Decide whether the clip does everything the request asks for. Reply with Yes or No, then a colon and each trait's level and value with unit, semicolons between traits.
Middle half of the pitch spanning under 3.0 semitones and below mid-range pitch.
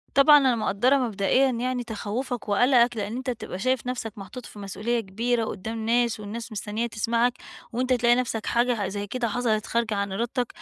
No: narrow, 2.6 semitones; high, 235 Hz